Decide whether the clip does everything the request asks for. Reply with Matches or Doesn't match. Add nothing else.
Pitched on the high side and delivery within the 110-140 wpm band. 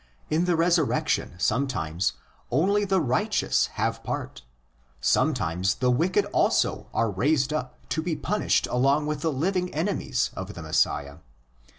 Doesn't match